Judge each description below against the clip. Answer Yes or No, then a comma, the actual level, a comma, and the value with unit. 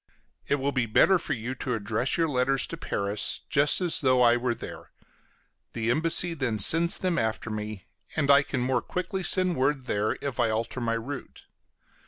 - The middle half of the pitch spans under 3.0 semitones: No, average, 4.9 semitones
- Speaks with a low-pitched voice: Yes, low, 130 Hz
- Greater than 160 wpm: Yes, average, 190 wpm